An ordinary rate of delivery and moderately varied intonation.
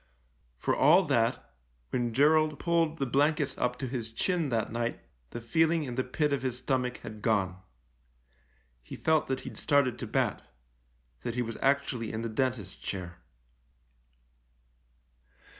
Yes: average, 155 wpm; average, 4.1 semitones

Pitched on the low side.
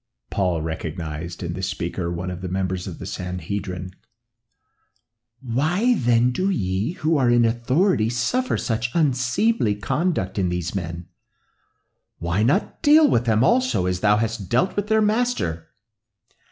Yes: low, 110 Hz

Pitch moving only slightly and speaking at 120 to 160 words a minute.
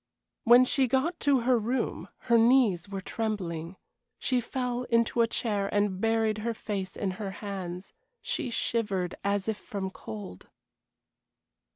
No: average, 3.8 semitones; average, 145 wpm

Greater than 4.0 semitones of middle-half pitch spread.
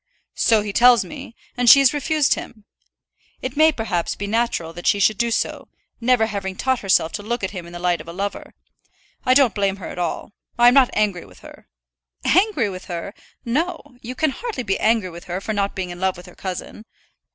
Yes: average, 5.2 semitones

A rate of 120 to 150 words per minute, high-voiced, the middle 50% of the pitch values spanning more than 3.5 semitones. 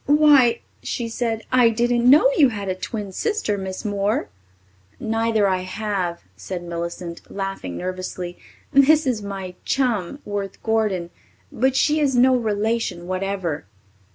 Yes: slow, 135 wpm; high, 210 Hz; average, 4.7 semitones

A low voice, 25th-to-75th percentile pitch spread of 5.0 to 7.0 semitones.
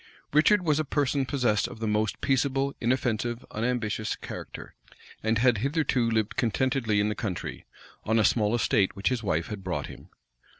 No: low, 115 Hz; average, 3.9 semitones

